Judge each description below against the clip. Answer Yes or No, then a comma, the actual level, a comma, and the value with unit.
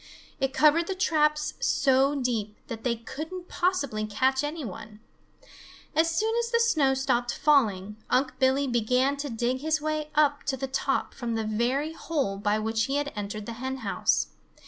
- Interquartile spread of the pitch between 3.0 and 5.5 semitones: Yes, average, 4.8 semitones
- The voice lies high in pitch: Yes, very high, 265 Hz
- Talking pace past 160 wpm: Yes, average, 175 wpm